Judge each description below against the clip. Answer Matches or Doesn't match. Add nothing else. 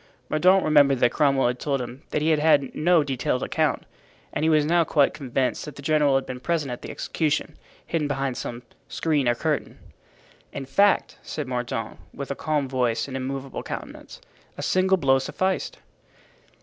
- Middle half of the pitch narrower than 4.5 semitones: Matches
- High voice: Doesn't match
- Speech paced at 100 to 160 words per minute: Doesn't match